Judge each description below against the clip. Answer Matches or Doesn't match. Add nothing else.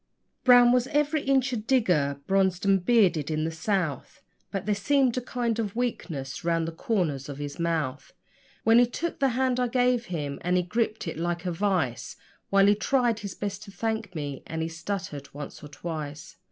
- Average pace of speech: Matches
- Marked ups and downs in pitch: Matches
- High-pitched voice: Matches